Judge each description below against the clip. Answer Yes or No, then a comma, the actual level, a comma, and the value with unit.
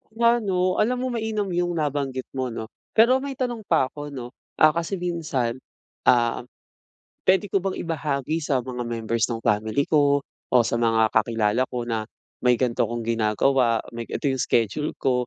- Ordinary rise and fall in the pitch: No, wide, 6.9 semitones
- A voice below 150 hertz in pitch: Yes, low, 135 Hz